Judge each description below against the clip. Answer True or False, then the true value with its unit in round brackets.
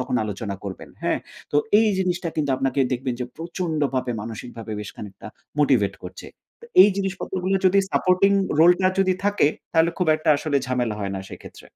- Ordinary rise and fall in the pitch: False (7.7 semitones)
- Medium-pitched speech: True (145 Hz)